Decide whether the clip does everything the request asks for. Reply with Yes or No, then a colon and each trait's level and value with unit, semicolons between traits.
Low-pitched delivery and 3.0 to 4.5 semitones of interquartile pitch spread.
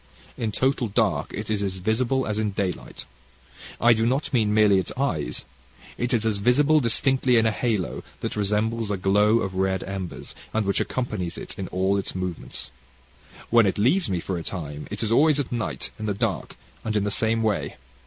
Yes: low, 105 Hz; average, 3.4 semitones